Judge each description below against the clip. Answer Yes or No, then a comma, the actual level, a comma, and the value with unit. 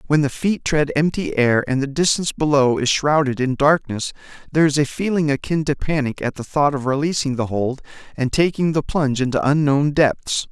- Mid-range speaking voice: Yes, medium, 145 Hz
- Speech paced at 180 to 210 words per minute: Yes, average, 200 wpm